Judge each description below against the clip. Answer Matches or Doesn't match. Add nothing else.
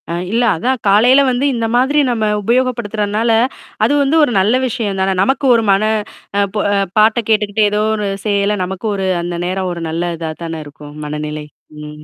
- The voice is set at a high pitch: Matches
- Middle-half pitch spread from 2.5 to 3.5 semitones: Doesn't match